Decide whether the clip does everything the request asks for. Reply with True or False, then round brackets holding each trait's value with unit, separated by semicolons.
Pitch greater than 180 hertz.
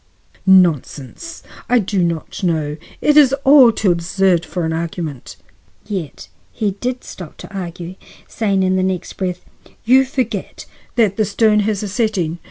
True (190 Hz)